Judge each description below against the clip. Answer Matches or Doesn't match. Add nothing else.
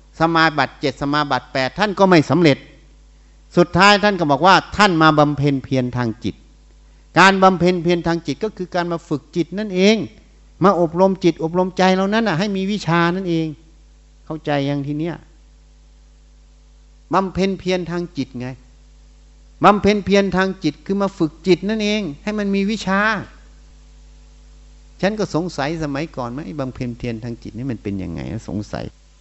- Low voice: Doesn't match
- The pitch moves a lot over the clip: Matches